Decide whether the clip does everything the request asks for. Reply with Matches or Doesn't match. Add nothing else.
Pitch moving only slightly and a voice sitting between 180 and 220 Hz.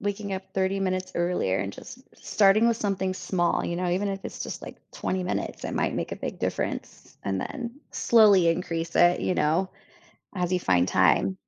Matches